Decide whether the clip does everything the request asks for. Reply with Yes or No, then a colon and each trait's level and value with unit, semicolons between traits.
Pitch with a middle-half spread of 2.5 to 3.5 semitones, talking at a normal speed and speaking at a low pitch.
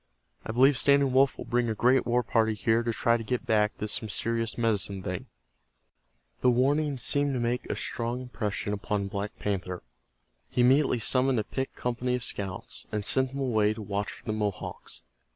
Yes: average, 3.2 semitones; average, 190 wpm; low, 115 Hz